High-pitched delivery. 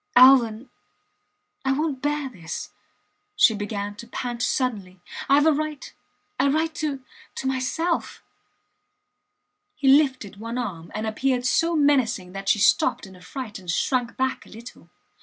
Yes: very high, 255 Hz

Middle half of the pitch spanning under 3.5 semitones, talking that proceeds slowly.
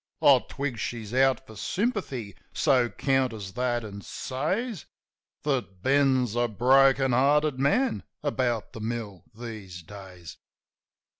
No: average, 3.9 semitones; slow, 120 wpm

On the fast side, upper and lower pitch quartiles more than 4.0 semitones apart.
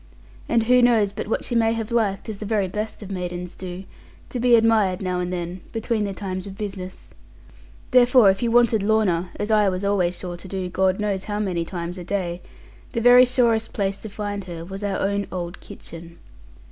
No: fast, 210 wpm; average, 3.3 semitones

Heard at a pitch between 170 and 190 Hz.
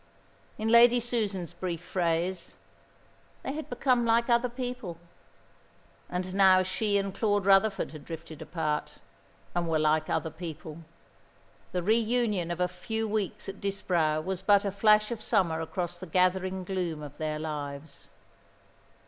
Yes: medium, 185 Hz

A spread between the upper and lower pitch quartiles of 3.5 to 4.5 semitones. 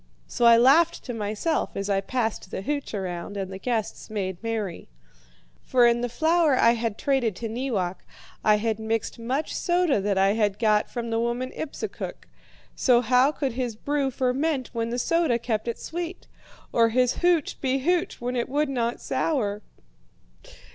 Yes: average, 3.9 semitones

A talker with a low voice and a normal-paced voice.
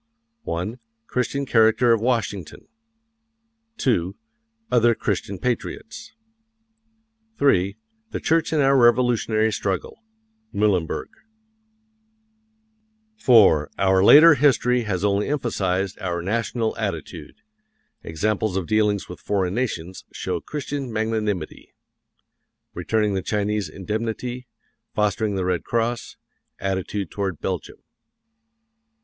No: low, 105 Hz; slow, 95 wpm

